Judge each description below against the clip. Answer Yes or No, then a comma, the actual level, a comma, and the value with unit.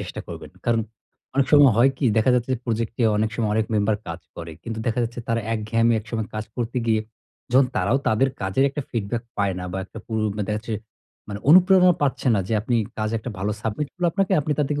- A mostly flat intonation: No, average, 3.7 semitones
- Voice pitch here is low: Yes, low, 115 Hz